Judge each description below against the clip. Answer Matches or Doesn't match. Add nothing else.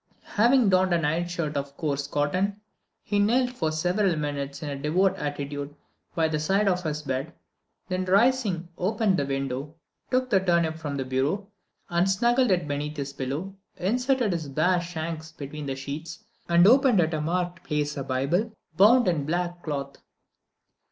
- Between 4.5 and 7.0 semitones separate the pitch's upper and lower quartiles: Matches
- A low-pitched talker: Doesn't match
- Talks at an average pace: Matches